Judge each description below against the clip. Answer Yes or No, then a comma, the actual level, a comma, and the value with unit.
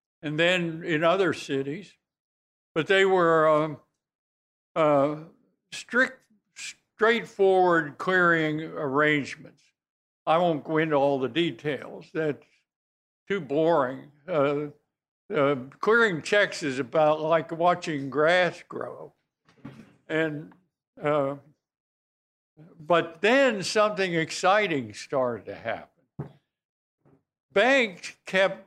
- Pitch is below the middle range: No, medium, 160 Hz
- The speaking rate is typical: No, slow, 95 wpm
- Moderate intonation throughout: Yes, average, 4.0 semitones